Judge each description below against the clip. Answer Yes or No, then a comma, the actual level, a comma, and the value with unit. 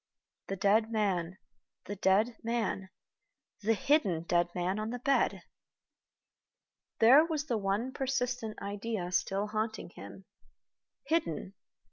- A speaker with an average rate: No, slow, 115 wpm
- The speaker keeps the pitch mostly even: No, average, 3.8 semitones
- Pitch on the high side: Yes, high, 215 Hz